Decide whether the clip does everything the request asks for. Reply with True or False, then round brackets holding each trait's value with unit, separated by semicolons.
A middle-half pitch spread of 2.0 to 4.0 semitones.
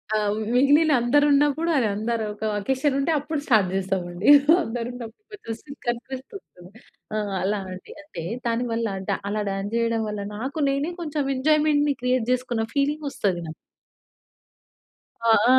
False (5.0 semitones)